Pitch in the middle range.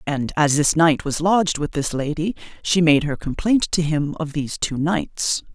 Yes: medium, 155 Hz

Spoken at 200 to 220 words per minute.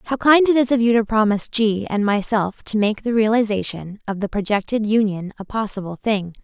Yes: fast, 205 wpm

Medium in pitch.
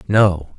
No: very low, 95 Hz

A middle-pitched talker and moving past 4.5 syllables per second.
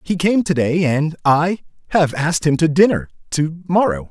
Yes: medium, 160 Hz; 4.8 syllables/s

